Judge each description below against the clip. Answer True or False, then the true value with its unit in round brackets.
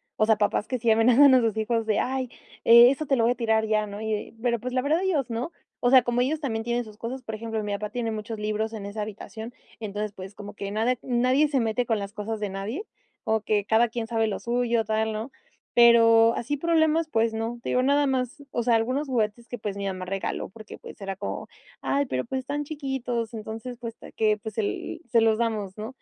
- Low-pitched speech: False (230 Hz)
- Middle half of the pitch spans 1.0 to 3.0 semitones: True (2.7 semitones)